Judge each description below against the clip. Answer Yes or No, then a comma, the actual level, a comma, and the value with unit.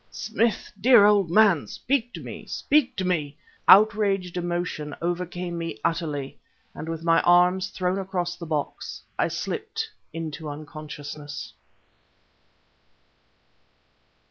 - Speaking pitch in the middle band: Yes, medium, 175 Hz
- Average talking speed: No, slow, 115 wpm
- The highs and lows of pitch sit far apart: No, average, 3.7 semitones